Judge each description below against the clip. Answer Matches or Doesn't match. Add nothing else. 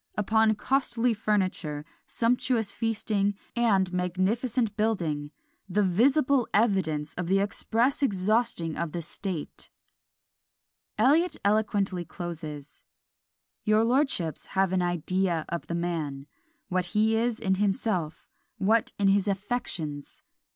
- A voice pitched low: Doesn't match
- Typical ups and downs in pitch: Matches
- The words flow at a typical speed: Doesn't match